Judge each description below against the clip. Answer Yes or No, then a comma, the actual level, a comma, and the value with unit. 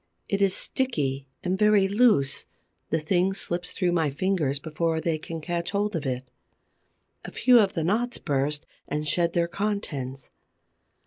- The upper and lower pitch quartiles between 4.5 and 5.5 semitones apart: Yes, average, 4.9 semitones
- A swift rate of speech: No, average, 155 wpm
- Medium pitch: Yes, medium, 170 Hz